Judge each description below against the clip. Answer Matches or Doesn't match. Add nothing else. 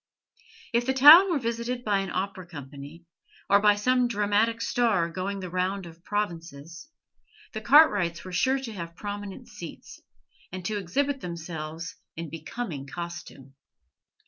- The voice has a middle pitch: Doesn't match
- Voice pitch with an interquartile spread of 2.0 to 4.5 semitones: Doesn't match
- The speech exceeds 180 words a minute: Doesn't match